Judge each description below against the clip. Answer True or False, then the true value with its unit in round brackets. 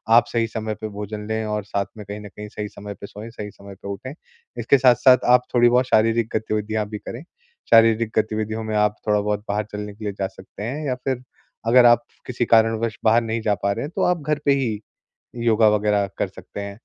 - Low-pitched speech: True (110 Hz)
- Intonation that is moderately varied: False (2.1 semitones)